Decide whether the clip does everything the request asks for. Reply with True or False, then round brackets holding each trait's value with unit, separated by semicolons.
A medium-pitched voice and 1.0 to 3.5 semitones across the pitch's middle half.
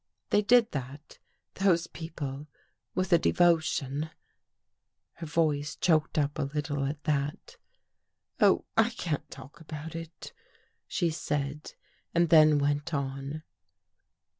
True (155 Hz; 2.6 semitones)